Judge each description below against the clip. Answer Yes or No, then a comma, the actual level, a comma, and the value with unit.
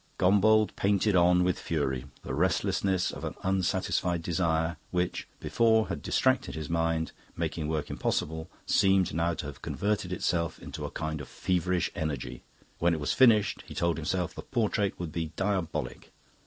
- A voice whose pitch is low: Yes, very low, 85 Hz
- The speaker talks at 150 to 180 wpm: Yes, average, 160 wpm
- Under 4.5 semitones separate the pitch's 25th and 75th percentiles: Yes, average, 3.2 semitones